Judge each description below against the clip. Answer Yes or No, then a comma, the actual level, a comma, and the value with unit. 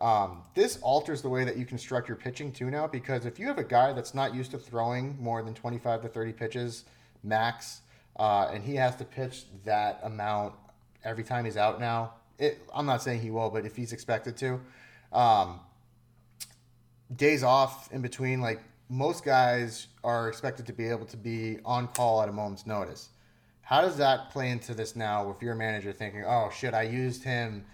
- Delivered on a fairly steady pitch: Yes, narrow, 2.3 semitones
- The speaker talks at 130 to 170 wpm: No, average, 195 wpm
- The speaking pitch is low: Yes, low, 120 Hz